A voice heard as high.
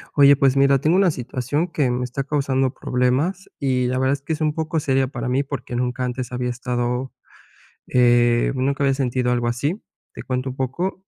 No: low, 130 Hz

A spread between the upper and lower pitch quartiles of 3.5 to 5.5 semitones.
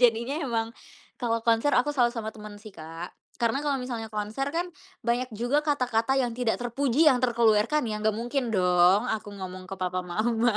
No: average, 2.9 semitones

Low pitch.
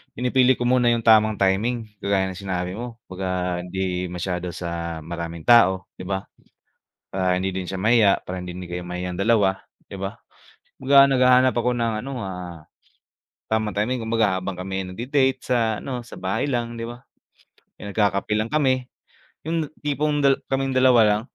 Yes: low, 105 Hz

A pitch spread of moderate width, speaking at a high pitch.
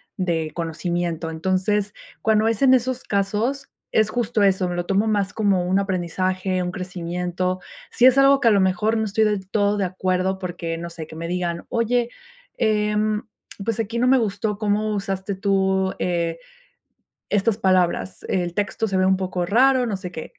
Yes: average, 3.1 semitones; high, 195 Hz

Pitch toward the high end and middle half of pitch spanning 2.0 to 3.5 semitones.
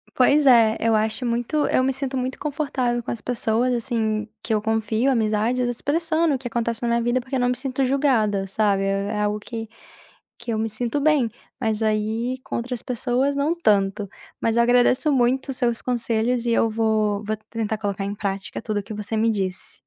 Yes: high, 235 Hz; average, 2.9 semitones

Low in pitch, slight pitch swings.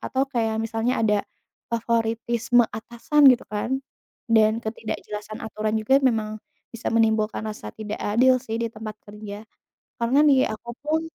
No: high, 225 Hz; narrow, 1.7 semitones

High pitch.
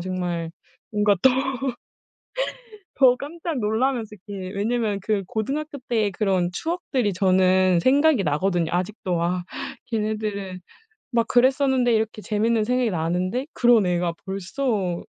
Yes: high, 210 Hz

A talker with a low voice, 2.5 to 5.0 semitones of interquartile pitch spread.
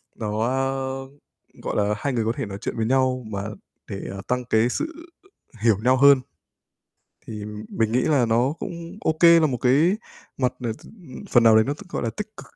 Yes: low, 125 Hz; average, 3.5 semitones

